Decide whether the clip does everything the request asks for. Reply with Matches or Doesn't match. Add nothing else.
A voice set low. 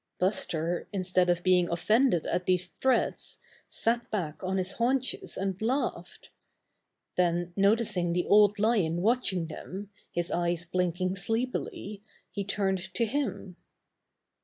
Doesn't match